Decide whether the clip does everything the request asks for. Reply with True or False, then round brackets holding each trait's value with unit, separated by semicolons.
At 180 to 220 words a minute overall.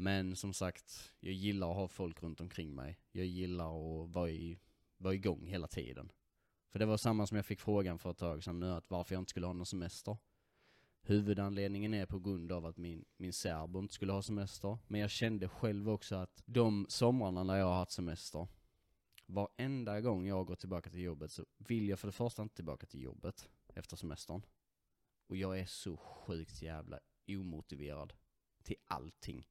True (190 wpm)